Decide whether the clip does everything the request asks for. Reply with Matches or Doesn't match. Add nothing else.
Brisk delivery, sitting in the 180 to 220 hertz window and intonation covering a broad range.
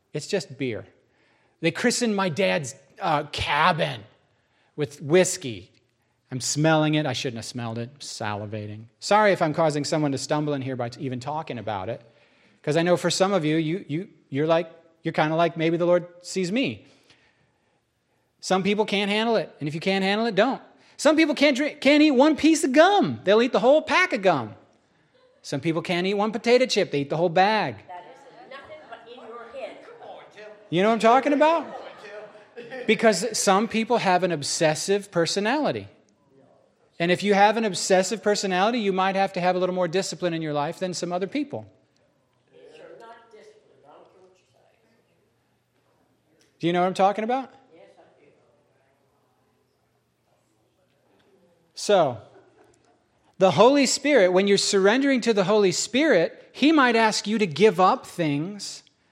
Doesn't match